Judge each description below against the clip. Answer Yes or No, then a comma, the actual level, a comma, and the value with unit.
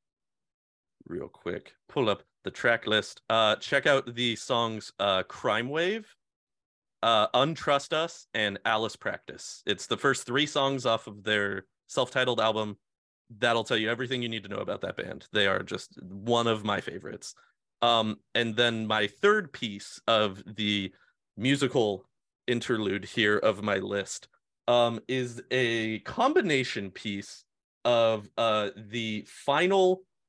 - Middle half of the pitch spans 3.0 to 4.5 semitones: Yes, average, 3.5 semitones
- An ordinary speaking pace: Yes, average, 145 wpm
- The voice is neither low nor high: No, low, 115 Hz